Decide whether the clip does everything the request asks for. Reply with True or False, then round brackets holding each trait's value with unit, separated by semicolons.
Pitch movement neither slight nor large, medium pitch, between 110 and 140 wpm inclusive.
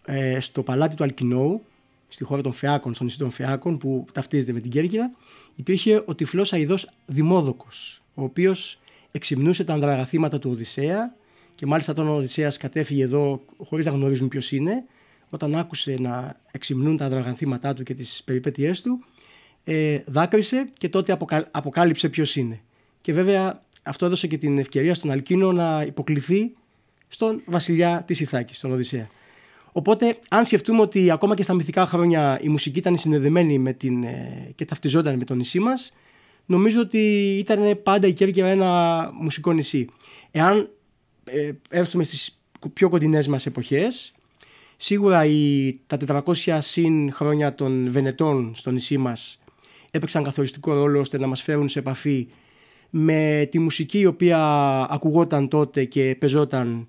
False (4.6 semitones; 150 Hz; 150 wpm)